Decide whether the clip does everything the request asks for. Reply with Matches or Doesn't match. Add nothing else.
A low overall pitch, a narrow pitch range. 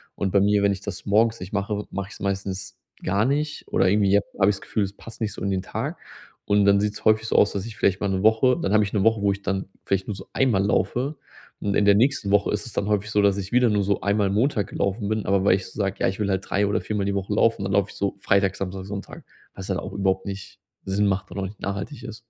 Matches